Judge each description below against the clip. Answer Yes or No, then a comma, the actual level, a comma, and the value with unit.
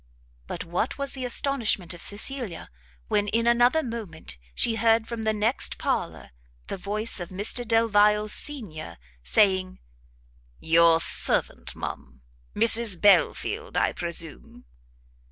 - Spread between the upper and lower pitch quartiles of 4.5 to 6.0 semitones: Yes, average, 4.9 semitones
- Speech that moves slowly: Yes, slow, 120 wpm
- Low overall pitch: No, high, 210 Hz